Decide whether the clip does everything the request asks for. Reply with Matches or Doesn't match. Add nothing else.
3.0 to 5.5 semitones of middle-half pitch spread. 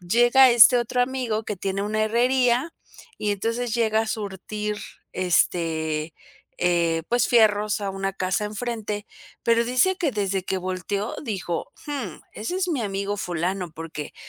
Matches